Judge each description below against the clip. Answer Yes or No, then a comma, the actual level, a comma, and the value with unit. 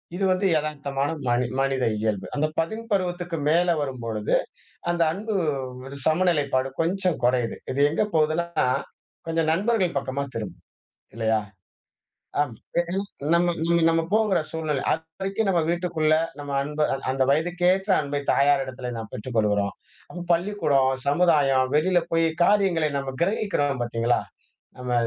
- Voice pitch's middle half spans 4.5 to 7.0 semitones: Yes, average, 5.0 semitones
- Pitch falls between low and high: Yes, medium, 155 Hz